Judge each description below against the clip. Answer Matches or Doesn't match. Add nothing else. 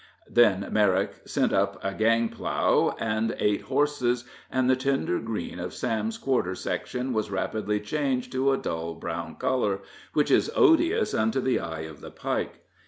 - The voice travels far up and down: Doesn't match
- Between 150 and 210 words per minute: Matches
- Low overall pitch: Matches